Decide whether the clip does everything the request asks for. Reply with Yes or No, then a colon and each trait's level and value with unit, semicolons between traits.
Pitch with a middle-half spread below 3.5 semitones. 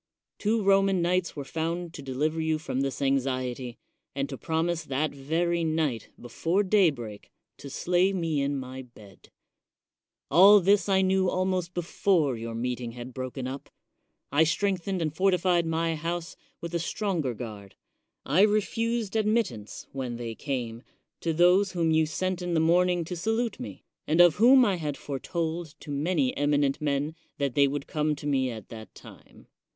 No: average, 5.1 semitones